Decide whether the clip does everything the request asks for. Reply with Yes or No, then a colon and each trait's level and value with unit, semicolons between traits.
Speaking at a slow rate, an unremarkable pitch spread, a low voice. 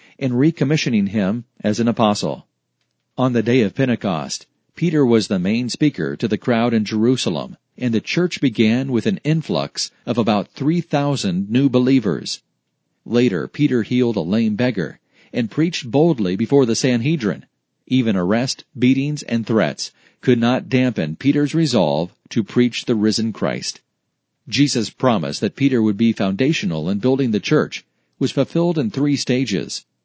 No: average, 150 wpm; average, 4.4 semitones; low, 130 Hz